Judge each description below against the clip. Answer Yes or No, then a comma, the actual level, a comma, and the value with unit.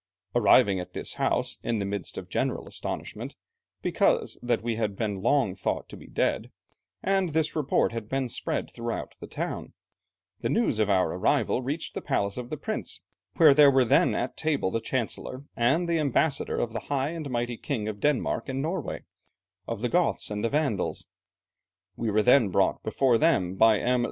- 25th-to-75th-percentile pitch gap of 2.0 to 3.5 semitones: No, average, 5.2 semitones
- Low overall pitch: Yes, low, 120 Hz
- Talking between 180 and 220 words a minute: Yes, average, 185 wpm